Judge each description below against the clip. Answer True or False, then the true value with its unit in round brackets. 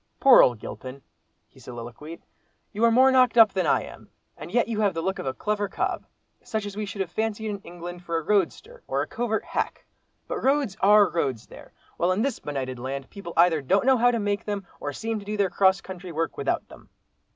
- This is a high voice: True (195 Hz)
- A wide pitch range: False (4.9 semitones)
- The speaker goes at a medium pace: False (220 wpm)